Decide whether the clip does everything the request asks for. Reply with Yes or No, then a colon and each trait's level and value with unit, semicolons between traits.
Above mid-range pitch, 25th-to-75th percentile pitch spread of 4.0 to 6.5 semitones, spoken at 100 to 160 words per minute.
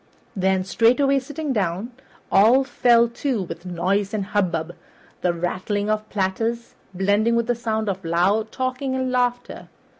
Yes: high, 215 Hz; average, 4.4 semitones; average, 145 wpm